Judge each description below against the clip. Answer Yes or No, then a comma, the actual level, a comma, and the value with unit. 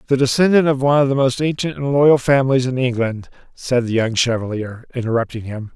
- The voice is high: No, low, 130 Hz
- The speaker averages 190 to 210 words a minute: Yes, average, 200 wpm